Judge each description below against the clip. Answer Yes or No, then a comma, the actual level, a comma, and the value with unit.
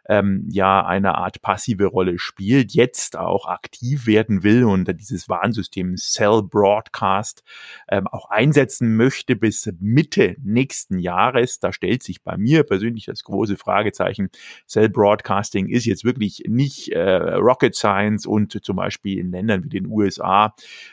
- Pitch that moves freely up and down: No, average, 3.3 semitones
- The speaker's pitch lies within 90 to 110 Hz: Yes, low, 105 Hz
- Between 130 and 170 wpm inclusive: Yes, average, 140 wpm